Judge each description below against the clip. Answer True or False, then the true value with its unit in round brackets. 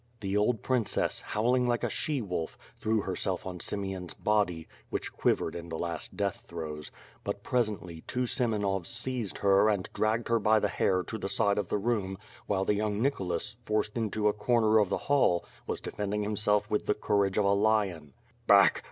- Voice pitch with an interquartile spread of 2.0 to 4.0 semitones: True (2.6 semitones)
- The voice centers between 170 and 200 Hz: False (105 Hz)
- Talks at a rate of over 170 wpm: True (185 wpm)